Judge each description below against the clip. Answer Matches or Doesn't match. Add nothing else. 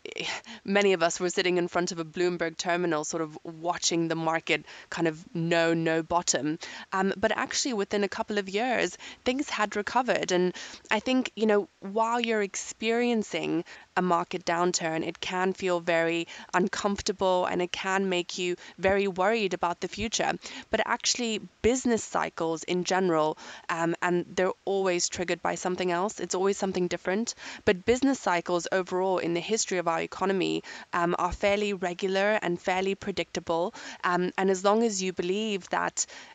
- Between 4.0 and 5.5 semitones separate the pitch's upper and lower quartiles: Doesn't match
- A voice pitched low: Doesn't match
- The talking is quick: Doesn't match